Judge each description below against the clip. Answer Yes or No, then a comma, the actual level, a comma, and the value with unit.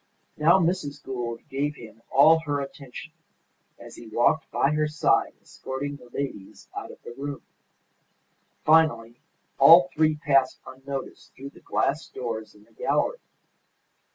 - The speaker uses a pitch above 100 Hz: Yes, medium, 140 Hz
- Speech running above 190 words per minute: No, average, 140 wpm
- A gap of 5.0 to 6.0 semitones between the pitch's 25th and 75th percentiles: No, average, 3.7 semitones